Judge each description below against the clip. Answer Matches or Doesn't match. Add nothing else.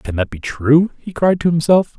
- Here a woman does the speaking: Doesn't match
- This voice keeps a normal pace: Doesn't match